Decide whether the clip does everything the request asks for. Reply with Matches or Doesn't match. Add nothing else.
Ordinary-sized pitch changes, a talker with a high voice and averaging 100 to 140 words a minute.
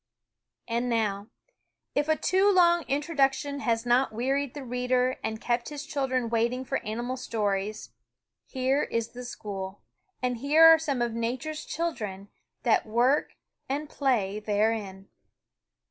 Matches